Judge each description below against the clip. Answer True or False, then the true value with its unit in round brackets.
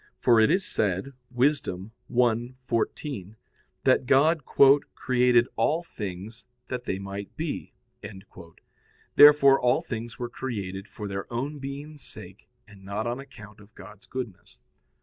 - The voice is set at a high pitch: False (120 Hz)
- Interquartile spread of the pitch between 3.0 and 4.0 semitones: False (4.8 semitones)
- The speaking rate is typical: False (130 wpm)